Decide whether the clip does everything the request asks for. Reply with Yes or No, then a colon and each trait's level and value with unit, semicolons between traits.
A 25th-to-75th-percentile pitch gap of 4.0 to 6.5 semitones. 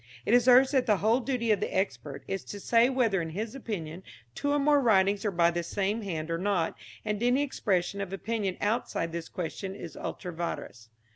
Yes: average, 5.2 semitones